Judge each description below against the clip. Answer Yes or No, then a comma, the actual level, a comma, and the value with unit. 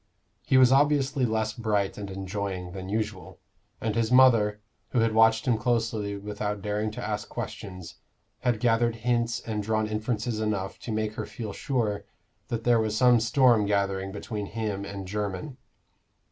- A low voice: Yes, low, 110 Hz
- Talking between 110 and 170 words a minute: Yes, average, 160 wpm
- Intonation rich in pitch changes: No, narrow, 2.4 semitones